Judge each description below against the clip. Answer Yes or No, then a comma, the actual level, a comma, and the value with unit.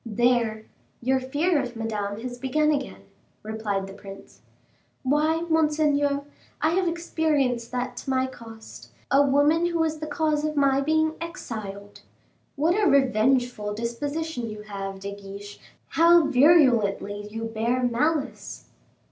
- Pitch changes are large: Yes, wide, 5.7 semitones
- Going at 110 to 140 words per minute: Yes, slow, 135 wpm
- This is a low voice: No, very high, 260 Hz